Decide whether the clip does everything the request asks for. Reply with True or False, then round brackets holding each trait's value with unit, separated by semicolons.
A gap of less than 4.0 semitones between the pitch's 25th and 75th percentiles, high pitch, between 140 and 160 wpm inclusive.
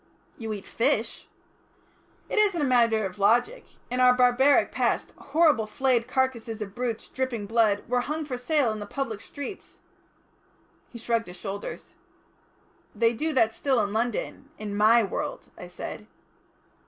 True (3.4 semitones; 235 Hz; 155 wpm)